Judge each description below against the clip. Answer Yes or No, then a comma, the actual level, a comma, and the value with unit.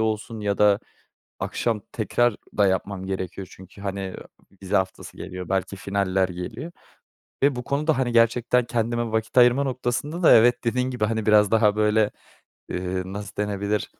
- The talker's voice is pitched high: No, low, 105 Hz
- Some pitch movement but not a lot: Yes, average, 3.7 semitones